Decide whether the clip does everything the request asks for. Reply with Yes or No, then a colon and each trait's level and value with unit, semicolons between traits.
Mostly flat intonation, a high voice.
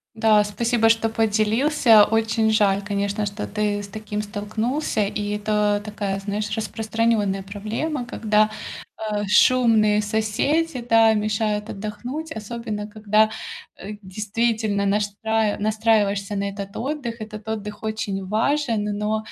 Yes: narrow, 1.4 semitones; high, 215 Hz